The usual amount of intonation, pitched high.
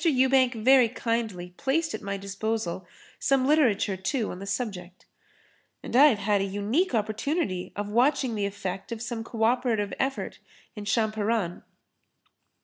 Yes: average, 4.4 semitones; high, 220 Hz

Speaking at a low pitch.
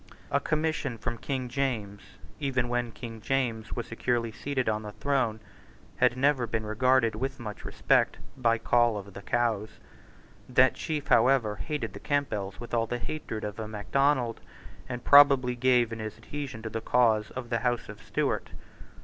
Yes: low, 120 Hz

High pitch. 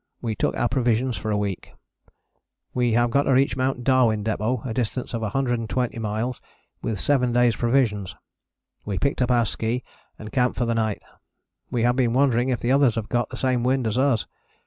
No: low, 120 Hz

